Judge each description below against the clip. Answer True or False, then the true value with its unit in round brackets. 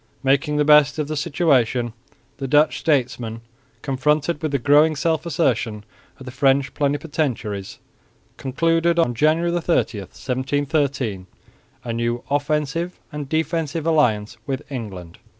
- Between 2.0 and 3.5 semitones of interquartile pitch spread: False (4.0 semitones)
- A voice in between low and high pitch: True (145 Hz)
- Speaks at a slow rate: True (125 wpm)